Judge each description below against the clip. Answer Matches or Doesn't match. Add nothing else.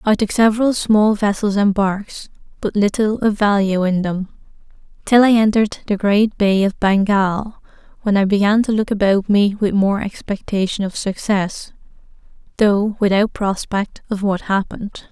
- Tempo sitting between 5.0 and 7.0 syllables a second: Doesn't match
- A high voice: Matches